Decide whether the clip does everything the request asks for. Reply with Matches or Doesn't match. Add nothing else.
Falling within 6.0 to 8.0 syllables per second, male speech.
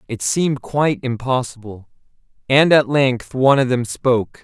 Doesn't match